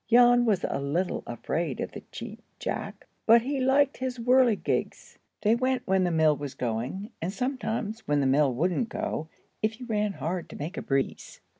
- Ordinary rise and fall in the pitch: No, wide, 8.0 semitones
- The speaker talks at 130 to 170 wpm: No, average, 185 wpm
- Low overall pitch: No, high, 210 Hz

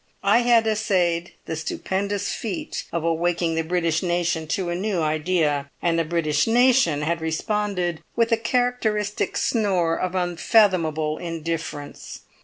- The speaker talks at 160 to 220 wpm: No, slow, 135 wpm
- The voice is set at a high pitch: No, medium, 175 Hz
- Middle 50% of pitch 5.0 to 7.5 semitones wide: No, average, 4.2 semitones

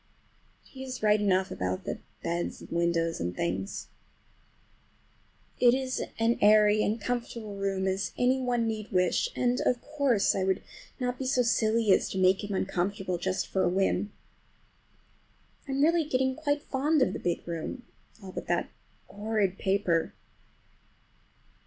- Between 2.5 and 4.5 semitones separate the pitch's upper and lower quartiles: No, average, 4.9 semitones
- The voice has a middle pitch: No, high, 210 Hz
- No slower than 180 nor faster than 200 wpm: No, average, 160 wpm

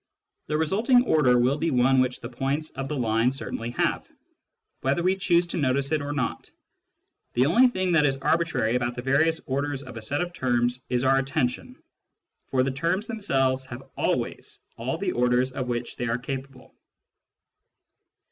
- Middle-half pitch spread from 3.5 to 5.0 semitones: Yes, average, 4.3 semitones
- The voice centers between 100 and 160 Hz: Yes, low, 135 Hz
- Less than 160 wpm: No, average, 175 wpm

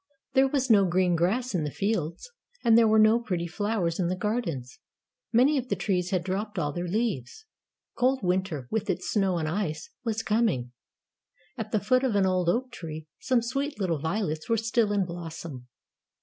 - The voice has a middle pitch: No, high, 195 Hz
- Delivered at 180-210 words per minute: Yes, average, 190 wpm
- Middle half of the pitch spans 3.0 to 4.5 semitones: No, average, 5.0 semitones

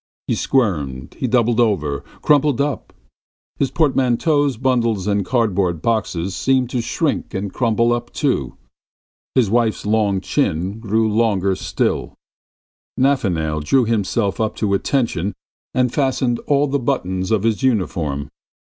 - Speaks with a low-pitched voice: Yes, low, 110 Hz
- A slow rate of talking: Yes, slow, 130 wpm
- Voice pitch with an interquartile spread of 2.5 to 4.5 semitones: No, average, 5.1 semitones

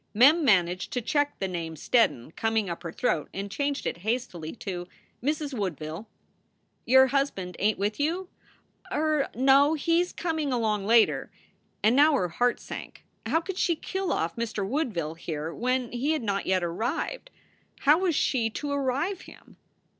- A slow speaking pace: No, average, 170 wpm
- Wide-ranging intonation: Yes, wide, 7.4 semitones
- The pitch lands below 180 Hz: No, high, 240 Hz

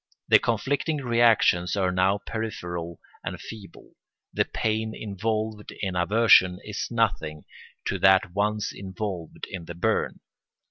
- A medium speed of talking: No, slow, 125 wpm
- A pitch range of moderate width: Yes, average, 3.4 semitones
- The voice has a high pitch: No, low, 100 Hz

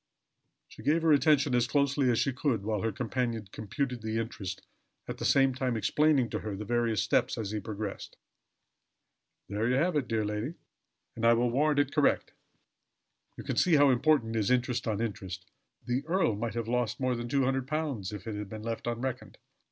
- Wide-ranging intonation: No, average, 3.9 semitones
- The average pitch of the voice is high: No, low, 120 Hz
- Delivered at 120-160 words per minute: No, average, 190 wpm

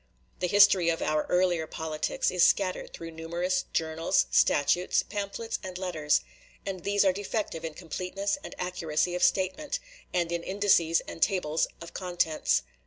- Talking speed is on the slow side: No, average, 150 wpm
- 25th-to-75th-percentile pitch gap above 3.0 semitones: No, average, 2.7 semitones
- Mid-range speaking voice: Yes, medium, 180 Hz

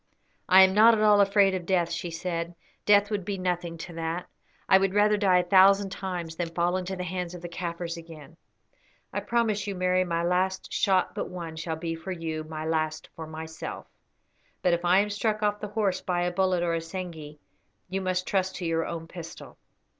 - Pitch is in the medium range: Yes, medium, 180 Hz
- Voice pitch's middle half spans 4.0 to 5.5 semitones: No, narrow, 2.5 semitones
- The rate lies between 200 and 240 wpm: Yes, fast, 205 wpm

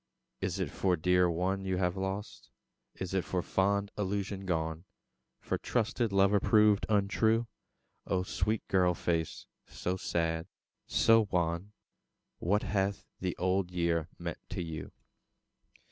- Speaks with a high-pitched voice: No, very low, 95 Hz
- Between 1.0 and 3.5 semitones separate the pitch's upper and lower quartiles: Yes, narrow, 2.4 semitones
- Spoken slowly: Yes, slow, 130 wpm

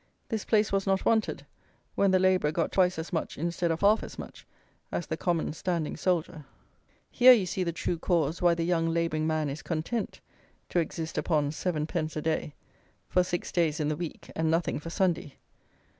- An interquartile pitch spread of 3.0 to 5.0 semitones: No, narrow, 2.5 semitones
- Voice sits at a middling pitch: Yes, medium, 170 Hz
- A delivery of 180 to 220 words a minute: Yes, average, 190 wpm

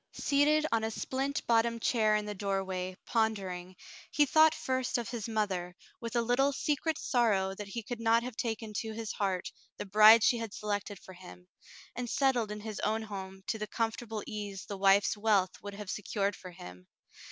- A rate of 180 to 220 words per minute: Yes, average, 195 wpm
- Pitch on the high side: Yes, high, 215 Hz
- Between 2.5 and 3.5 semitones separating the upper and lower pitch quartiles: Yes, average, 3.1 semitones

